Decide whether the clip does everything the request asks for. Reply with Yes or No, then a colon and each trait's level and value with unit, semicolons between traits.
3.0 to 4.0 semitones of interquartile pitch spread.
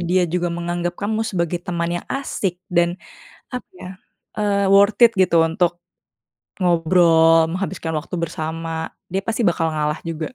No: narrow, 2.5 semitones